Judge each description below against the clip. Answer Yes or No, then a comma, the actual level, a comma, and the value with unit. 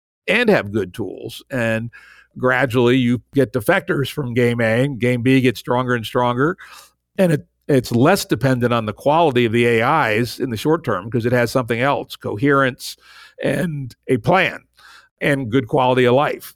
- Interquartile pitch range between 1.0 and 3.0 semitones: Yes, narrow, 2.6 semitones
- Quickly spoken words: No, average, 175 wpm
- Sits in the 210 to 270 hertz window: No, low, 130 Hz